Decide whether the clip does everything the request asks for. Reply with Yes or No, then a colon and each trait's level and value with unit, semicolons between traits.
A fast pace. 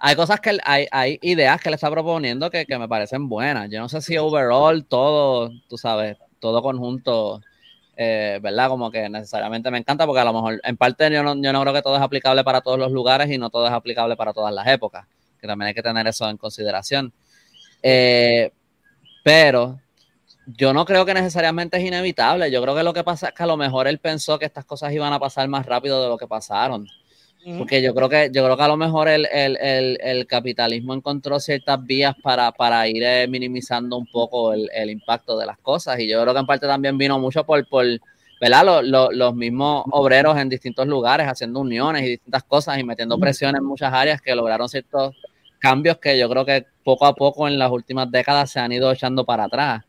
Yes: fast, 220 wpm